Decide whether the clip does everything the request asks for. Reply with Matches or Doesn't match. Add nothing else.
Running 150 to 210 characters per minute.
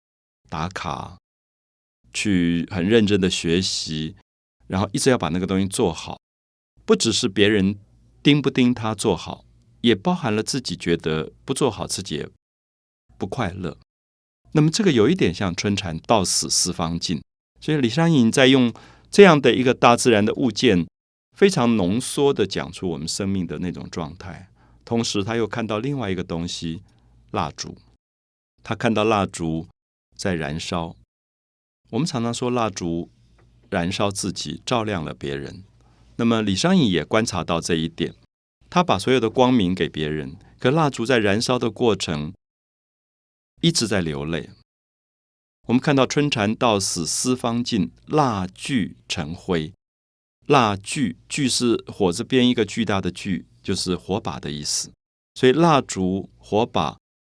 Doesn't match